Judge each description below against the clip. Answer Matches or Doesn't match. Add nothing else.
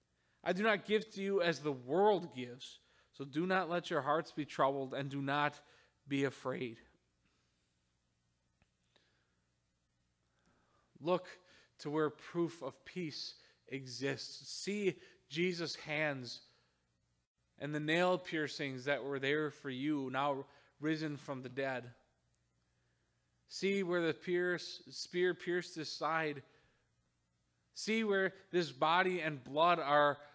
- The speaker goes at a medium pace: Doesn't match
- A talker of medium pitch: Matches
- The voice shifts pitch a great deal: Matches